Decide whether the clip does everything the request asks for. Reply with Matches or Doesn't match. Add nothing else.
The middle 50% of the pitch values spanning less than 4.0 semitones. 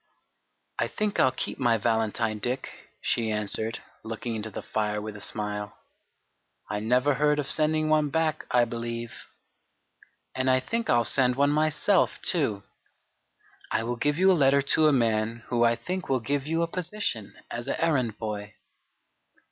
Doesn't match